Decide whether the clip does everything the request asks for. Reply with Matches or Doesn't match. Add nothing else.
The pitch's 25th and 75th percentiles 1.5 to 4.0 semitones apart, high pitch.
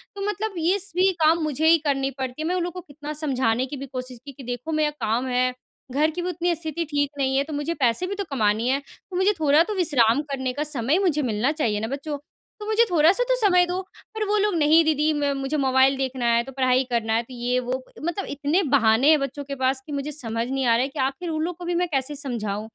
Doesn't match